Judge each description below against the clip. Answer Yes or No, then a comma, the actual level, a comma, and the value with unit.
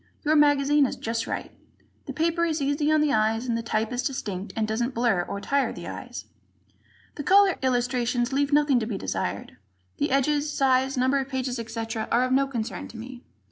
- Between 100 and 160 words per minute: No, average, 200 wpm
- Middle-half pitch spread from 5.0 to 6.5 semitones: No, average, 3.8 semitones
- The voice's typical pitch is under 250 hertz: No, very high, 255 Hz